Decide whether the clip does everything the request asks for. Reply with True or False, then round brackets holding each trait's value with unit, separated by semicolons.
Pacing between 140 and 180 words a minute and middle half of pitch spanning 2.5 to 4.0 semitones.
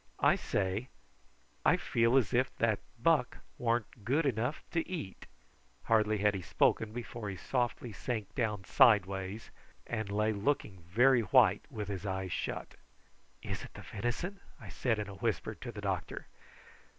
True (160 wpm; 3.4 semitones)